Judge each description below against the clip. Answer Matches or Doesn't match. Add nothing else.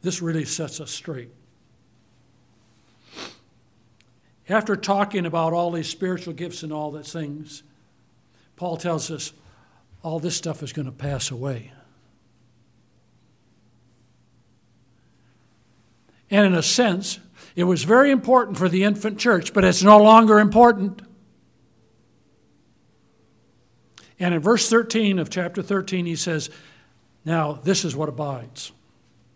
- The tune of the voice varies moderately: Doesn't match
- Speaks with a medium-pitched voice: Matches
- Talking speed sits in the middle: Doesn't match